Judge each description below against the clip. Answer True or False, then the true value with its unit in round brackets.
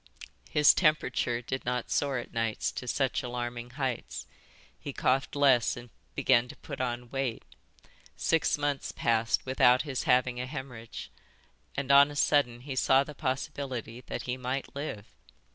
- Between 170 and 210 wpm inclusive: False (155 wpm)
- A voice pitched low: True (130 Hz)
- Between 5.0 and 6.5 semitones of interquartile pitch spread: False (2.5 semitones)